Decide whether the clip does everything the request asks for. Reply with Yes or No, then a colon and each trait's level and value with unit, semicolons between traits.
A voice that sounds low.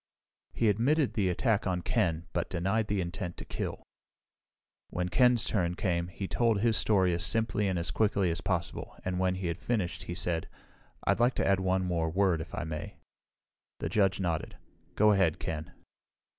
Yes: very low, 95 Hz